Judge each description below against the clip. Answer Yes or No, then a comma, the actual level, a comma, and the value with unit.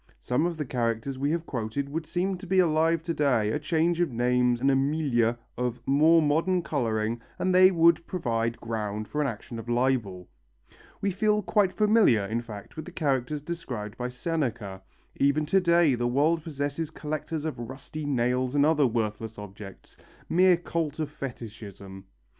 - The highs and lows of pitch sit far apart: Yes, wide, 5.8 semitones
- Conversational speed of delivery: Yes, average, 175 wpm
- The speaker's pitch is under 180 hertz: Yes, medium, 140 Hz